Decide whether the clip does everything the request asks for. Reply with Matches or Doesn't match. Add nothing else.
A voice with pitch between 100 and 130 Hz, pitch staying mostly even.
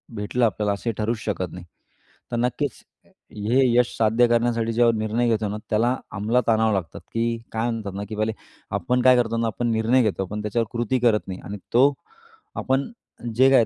Matches